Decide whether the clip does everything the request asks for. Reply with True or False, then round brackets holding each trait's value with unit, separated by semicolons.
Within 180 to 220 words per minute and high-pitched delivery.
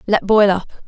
True (205 wpm; 195 Hz)